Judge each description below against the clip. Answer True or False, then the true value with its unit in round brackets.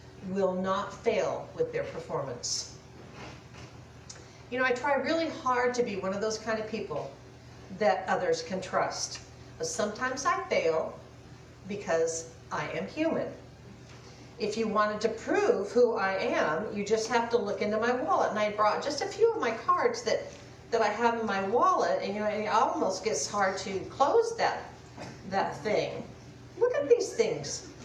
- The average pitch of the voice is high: True (215 Hz)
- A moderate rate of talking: True (170 wpm)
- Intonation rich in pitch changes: True (8.3 semitones)